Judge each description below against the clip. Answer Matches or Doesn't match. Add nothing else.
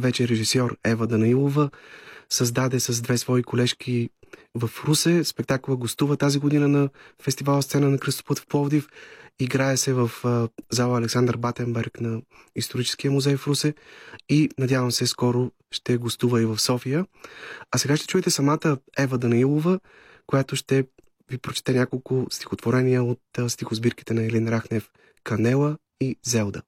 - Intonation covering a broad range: Doesn't match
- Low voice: Matches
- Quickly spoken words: Doesn't match